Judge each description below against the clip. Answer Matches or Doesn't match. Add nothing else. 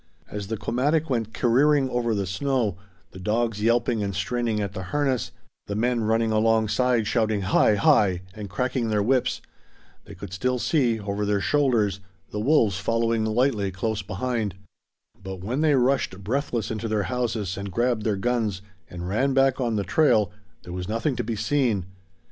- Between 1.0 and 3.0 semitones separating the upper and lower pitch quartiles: Doesn't match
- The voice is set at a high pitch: Doesn't match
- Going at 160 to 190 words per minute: Matches